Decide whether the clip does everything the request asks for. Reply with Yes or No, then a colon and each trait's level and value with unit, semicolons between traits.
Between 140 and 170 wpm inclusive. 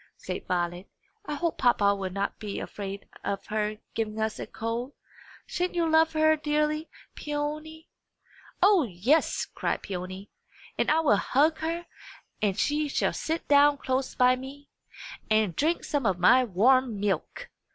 Yes: average, 150 wpm